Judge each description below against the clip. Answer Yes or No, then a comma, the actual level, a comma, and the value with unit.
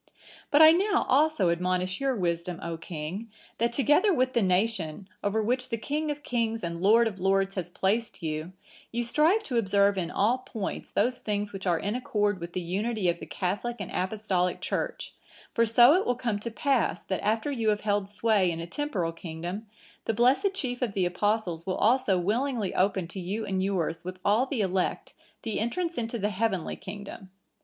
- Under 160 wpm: No, average, 195 wpm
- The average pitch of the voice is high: Yes, high, 205 Hz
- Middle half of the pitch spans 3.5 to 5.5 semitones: Yes, average, 4.6 semitones